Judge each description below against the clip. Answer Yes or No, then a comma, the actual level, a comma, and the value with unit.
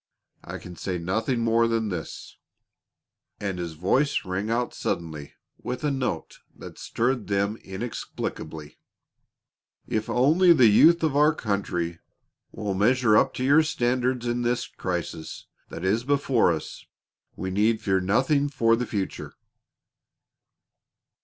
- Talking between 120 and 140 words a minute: Yes, slow, 135 wpm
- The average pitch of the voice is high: No, low, 115 Hz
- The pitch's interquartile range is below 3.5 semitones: No, average, 5.2 semitones